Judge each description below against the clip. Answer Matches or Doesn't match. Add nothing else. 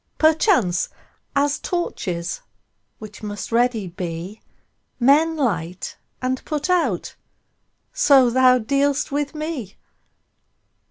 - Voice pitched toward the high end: Matches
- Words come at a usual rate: Doesn't match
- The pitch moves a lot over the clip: Matches